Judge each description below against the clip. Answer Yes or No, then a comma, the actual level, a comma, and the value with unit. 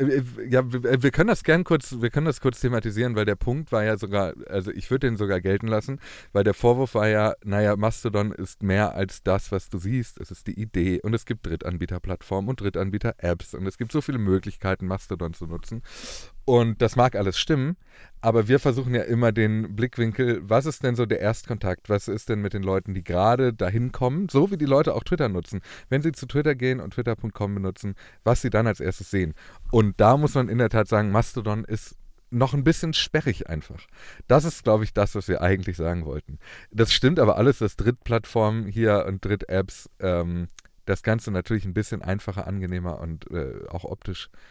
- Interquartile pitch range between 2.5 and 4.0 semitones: No, average, 4.4 semitones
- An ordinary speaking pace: No, fast, 205 wpm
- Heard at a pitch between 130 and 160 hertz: No, low, 110 Hz